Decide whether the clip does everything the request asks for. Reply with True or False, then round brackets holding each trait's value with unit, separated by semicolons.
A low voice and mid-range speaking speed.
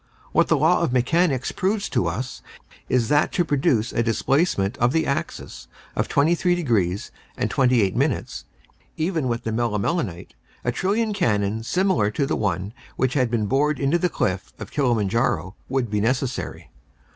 True (125 Hz; 160 wpm)